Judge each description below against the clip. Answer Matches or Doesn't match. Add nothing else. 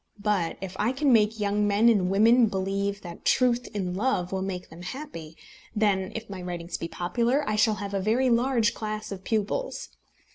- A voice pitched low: Doesn't match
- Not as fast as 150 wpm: Doesn't match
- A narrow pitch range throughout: Doesn't match